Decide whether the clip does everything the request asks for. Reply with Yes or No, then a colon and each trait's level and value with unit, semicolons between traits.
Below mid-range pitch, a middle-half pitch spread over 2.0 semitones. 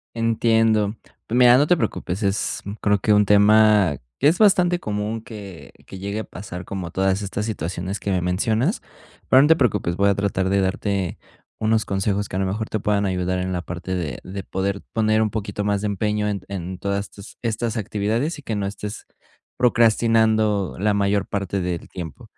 Yes: low, 100 Hz; narrow, 2.4 semitones